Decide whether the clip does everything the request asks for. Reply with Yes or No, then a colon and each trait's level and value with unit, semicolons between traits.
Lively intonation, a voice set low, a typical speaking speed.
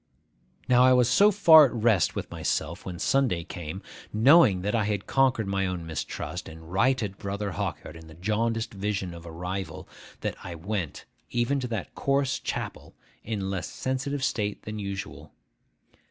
Yes: wide, 5.7 semitones; low, 105 Hz; average, 170 wpm